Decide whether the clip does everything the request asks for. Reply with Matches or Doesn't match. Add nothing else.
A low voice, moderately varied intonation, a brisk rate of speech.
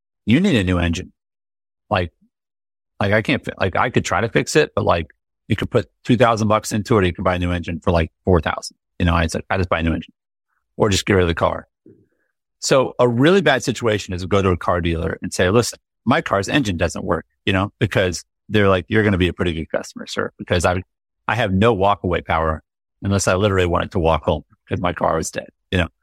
Matches